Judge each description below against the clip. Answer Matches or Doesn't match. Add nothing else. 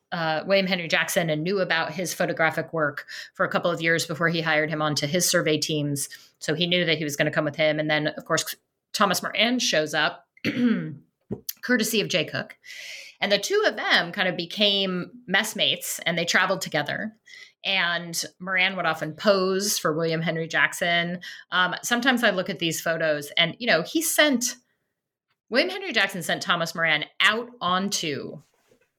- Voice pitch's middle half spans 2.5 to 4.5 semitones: Matches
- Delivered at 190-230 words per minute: Doesn't match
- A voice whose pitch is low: Doesn't match